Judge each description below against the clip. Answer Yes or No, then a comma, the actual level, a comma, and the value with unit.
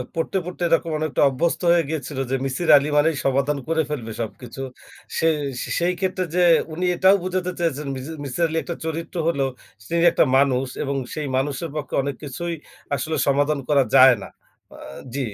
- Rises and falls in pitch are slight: No, average, 3.7 semitones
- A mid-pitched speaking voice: Yes, medium, 150 Hz